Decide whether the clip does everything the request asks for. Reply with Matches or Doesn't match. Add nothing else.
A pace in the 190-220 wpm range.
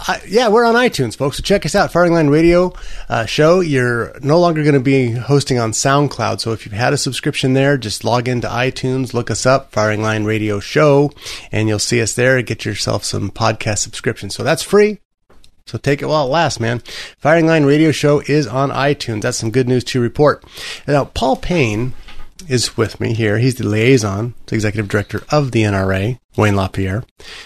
Matches